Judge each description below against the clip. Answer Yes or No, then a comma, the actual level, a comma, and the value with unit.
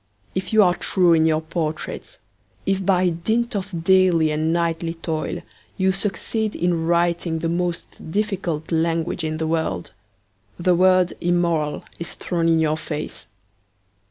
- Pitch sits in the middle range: Yes, medium, 170 Hz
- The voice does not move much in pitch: Yes, narrow, 2.3 semitones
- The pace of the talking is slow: No, average, 145 wpm